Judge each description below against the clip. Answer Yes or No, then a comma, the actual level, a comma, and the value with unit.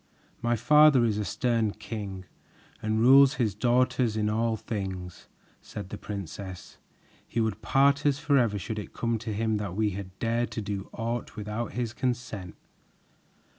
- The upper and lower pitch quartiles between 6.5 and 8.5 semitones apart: No, average, 2.8 semitones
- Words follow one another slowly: No, average, 160 wpm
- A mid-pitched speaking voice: No, low, 110 Hz